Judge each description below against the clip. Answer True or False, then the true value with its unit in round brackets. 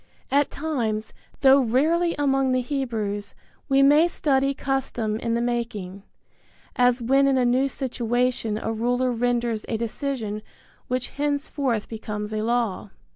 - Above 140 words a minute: False (135 wpm)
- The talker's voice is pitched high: True (245 Hz)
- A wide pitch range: False (3.4 semitones)